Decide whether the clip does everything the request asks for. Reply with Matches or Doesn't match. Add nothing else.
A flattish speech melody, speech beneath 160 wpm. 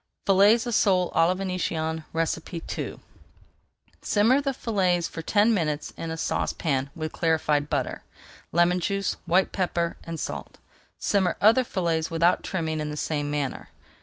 Doesn't match